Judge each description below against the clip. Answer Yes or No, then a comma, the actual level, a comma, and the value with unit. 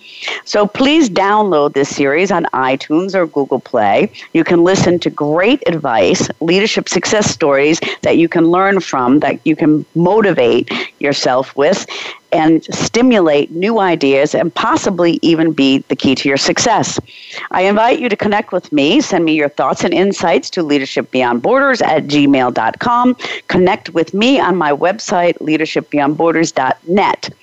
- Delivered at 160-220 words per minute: No, average, 145 wpm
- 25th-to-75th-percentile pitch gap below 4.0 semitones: No, average, 4.9 semitones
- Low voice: No, medium, 165 Hz